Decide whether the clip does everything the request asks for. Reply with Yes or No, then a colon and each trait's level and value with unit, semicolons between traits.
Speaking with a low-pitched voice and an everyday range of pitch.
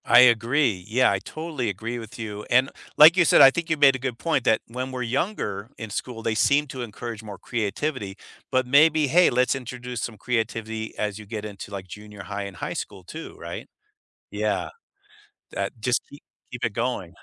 Yes: low, 120 Hz; average, 3.9 semitones